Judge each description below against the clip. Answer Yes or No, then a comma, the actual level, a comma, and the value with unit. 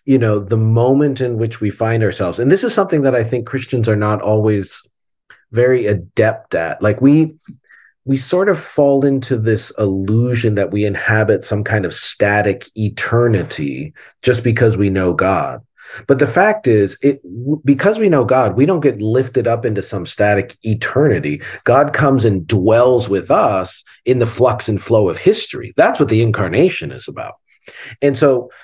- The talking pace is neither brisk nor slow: Yes, average, 175 wpm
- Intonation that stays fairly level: No, average, 4.2 semitones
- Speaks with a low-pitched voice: Yes, low, 120 Hz